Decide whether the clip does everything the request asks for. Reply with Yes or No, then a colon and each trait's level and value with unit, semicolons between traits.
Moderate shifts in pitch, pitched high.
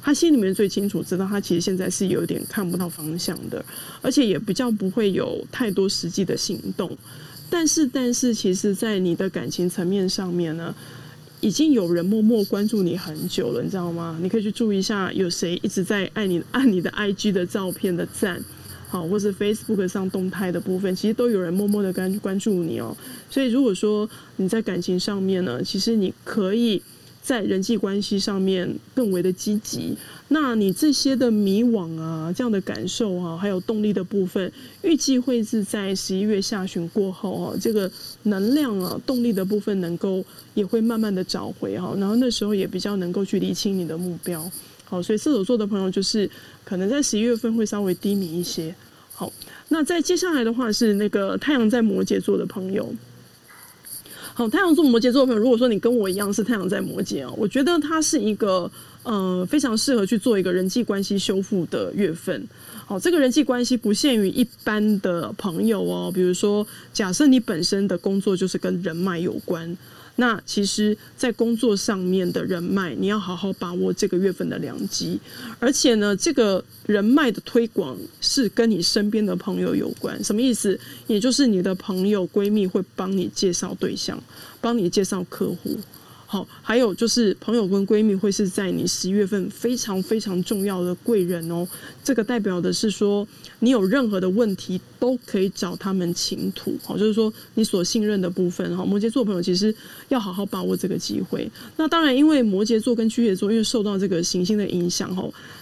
Yes: average, 3.6 semitones; high, 205 Hz